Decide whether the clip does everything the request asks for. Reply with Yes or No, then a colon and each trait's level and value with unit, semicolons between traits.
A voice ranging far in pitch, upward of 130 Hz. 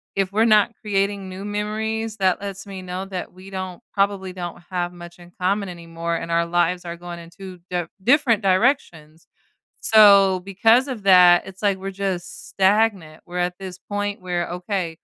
No: narrow, 2.5 semitones; high, 190 Hz